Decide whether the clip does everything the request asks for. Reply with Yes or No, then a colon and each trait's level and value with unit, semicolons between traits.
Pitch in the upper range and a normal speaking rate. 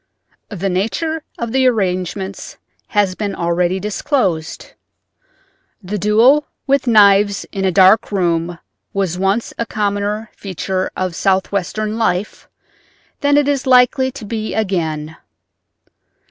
No: high, 200 Hz; slow, 120 wpm